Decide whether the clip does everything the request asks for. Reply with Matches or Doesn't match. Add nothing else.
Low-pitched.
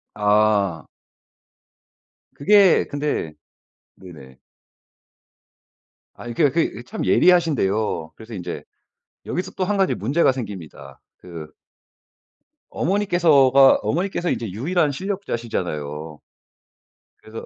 Matches